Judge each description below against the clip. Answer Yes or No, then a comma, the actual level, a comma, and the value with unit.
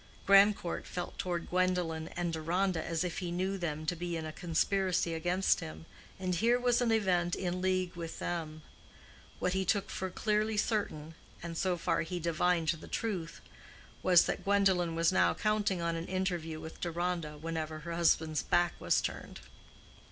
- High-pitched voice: No, medium, 175 Hz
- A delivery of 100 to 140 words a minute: No, average, 165 wpm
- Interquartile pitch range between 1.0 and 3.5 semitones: Yes, narrow, 2.4 semitones